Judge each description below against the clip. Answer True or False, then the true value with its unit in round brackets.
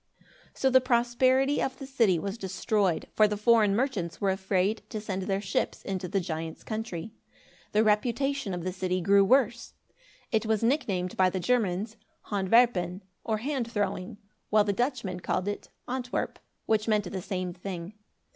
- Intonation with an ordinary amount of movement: True (4.1 semitones)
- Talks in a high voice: True (210 Hz)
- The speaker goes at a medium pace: True (165 wpm)